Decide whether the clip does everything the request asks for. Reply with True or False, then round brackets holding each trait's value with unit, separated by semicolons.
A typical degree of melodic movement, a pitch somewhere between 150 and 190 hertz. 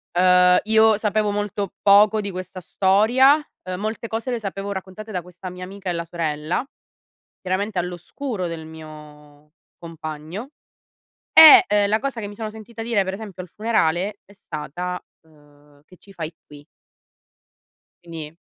True (4.2 semitones; 185 Hz)